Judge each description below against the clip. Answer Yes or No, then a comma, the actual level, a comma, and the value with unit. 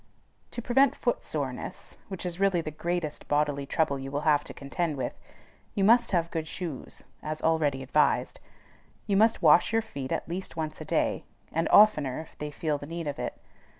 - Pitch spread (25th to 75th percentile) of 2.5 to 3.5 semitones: No, average, 4.1 semitones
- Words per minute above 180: Yes, average, 190 wpm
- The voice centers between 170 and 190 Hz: No, medium, 160 Hz